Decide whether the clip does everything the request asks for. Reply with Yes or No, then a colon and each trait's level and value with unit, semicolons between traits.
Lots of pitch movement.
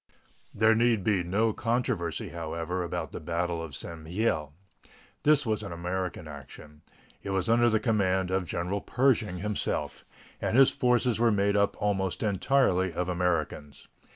No: average, 4.4 semitones